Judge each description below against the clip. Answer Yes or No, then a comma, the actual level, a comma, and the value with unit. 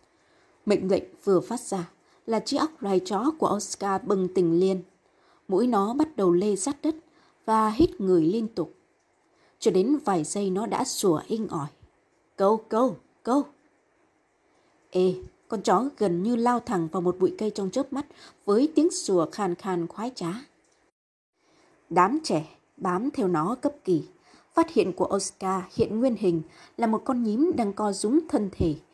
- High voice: Yes, high, 215 Hz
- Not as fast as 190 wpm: Yes, average, 170 wpm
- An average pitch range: No, wide, 7.5 semitones